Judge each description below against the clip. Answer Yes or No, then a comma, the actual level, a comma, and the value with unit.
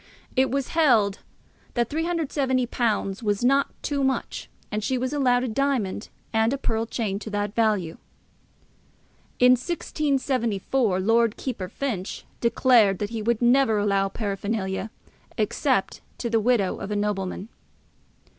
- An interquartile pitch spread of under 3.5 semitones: No, average, 4.1 semitones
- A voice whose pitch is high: Yes, high, 230 Hz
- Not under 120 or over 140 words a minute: Yes, slow, 135 wpm